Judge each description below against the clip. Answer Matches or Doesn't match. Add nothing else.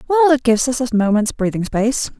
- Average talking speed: Doesn't match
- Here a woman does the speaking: Matches